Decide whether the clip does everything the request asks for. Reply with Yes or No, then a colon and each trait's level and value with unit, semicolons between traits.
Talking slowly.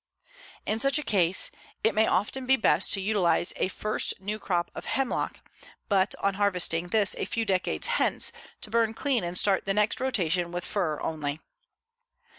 No: average, 175 wpm